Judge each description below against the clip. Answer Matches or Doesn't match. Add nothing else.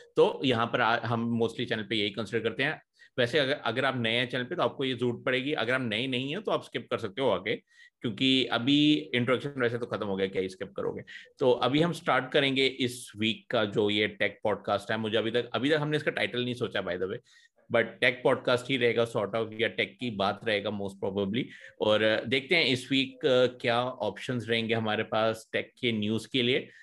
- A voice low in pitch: Matches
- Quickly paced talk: Matches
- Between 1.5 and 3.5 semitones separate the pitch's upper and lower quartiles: Matches